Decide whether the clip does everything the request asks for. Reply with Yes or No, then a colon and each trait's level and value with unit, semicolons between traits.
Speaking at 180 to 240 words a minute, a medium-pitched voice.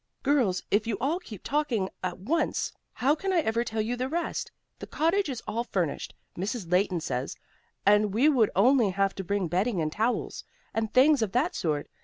No: average, 195 wpm; high, 220 Hz